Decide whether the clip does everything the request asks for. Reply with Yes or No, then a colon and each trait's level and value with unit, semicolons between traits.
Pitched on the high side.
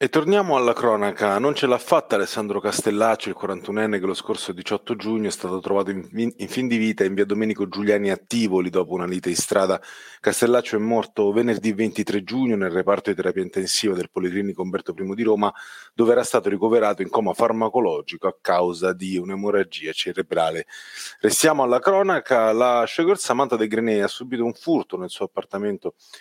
No: low, 110 Hz